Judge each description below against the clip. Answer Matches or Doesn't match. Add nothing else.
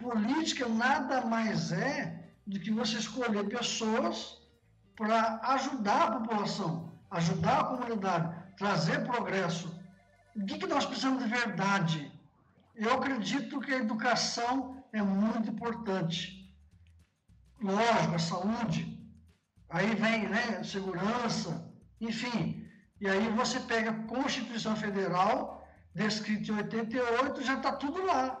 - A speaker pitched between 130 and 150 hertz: Doesn't match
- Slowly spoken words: Matches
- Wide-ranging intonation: Doesn't match